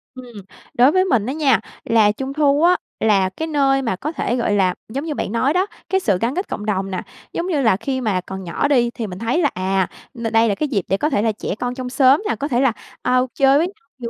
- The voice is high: Yes, very high, 250 Hz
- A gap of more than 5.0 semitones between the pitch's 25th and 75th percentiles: Yes, wide, 5.4 semitones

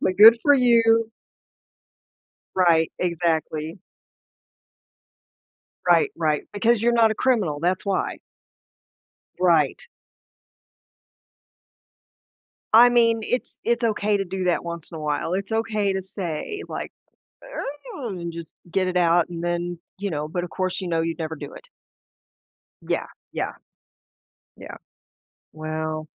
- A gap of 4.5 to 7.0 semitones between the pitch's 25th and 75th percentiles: Yes, average, 5.3 semitones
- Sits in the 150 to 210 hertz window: Yes, medium, 185 Hz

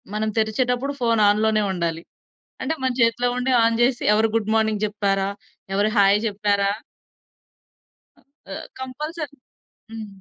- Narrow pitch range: No, average, 3.2 semitones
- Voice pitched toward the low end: No, high, 220 Hz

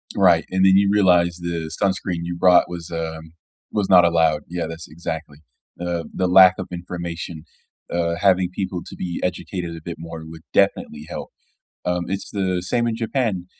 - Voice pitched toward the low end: Yes, very low, 90 Hz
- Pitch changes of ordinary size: No, narrow, 2.0 semitones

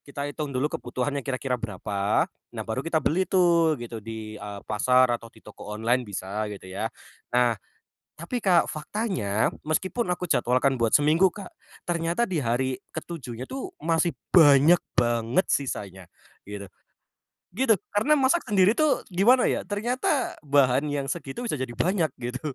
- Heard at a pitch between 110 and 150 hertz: Yes, medium, 140 Hz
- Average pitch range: No, wide, 7.2 semitones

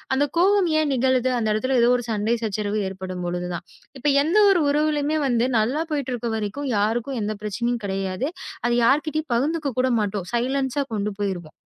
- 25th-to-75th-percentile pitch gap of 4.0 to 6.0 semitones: Yes, wide, 5.5 semitones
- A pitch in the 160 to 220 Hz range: No, high, 240 Hz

